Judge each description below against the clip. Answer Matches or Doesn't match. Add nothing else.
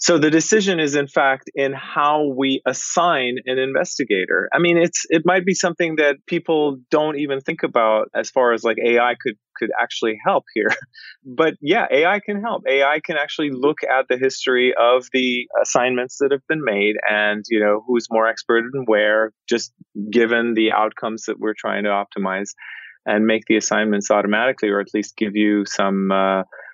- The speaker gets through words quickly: Doesn't match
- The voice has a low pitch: Matches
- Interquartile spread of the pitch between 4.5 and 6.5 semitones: Matches